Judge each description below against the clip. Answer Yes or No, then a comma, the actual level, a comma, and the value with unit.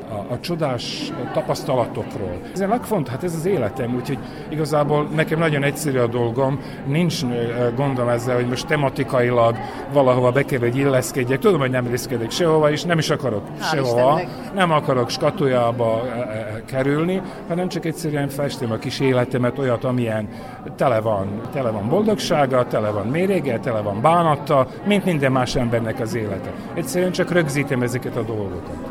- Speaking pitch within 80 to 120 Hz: No, low, 130 Hz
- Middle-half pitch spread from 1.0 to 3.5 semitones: No, average, 4.3 semitones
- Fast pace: Yes, fast, 160 wpm